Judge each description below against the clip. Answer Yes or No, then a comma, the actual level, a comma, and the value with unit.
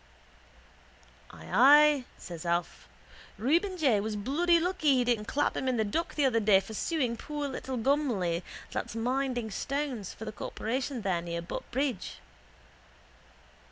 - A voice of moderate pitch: No, very high, 250 Hz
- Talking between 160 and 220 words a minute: No, average, 145 wpm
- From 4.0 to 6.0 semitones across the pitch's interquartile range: Yes, wide, 5.4 semitones